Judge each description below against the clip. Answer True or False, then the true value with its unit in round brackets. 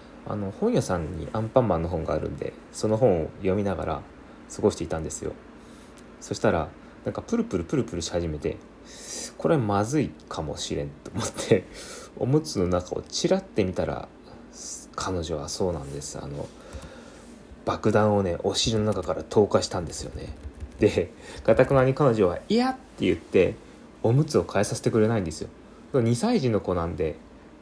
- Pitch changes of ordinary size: False (6.9 semitones)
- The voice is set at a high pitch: False (100 Hz)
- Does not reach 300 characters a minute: False (335 characters per minute)